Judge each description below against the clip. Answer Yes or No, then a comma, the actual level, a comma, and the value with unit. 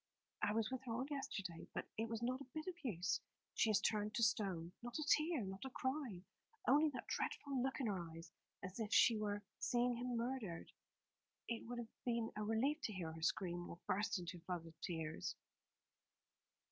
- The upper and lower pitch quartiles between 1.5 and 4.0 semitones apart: No, average, 5.2 semitones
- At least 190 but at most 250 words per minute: Yes, average, 200 wpm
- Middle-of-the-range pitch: No, high, 220 Hz